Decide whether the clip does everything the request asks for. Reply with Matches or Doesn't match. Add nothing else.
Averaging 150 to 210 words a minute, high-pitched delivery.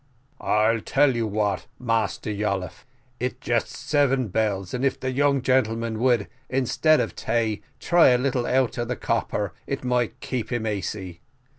Doesn't match